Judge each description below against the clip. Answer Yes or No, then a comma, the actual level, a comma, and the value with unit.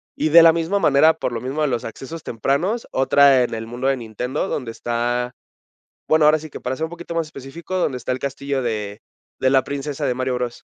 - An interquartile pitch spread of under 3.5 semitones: No, average, 4.2 semitones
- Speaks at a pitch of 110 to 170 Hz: Yes, low, 135 Hz